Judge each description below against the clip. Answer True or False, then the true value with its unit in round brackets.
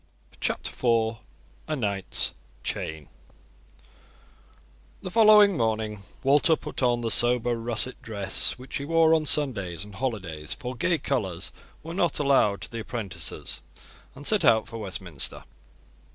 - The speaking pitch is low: True (120 Hz)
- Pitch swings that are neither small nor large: False (6.0 semitones)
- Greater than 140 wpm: False (135 wpm)